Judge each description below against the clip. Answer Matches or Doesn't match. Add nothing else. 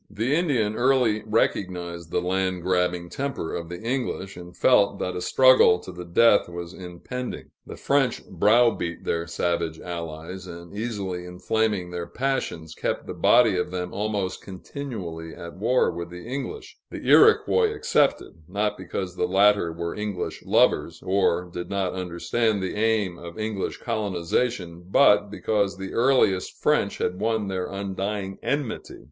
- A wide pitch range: Doesn't match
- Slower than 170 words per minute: Matches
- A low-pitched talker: Matches